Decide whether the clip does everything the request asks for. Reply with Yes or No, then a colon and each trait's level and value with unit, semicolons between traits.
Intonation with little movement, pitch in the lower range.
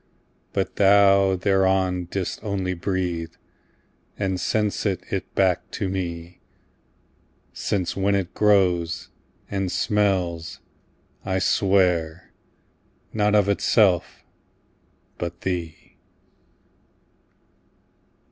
Yes: narrow, 2.0 semitones; very low, 95 Hz